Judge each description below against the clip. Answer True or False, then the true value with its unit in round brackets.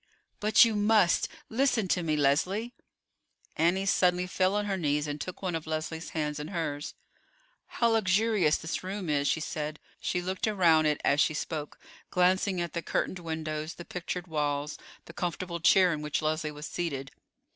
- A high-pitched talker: False (170 Hz)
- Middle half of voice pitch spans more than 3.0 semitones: True (3.6 semitones)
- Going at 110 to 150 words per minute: False (175 wpm)